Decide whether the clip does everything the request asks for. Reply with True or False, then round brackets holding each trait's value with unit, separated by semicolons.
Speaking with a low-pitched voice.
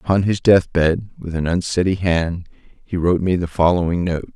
True (90 Hz)